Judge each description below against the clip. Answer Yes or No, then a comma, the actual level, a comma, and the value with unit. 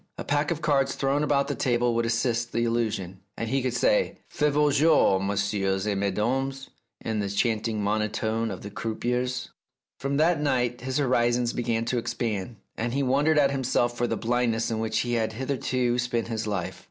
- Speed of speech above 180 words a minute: Yes, average, 190 wpm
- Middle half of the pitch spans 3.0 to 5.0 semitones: Yes, average, 3.3 semitones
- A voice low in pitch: Yes, low, 120 Hz